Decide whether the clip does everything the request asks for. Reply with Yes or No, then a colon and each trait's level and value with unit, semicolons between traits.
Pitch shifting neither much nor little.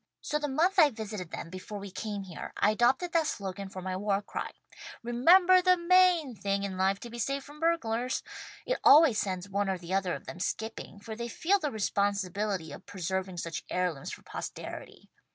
No: wide, 7.4 semitones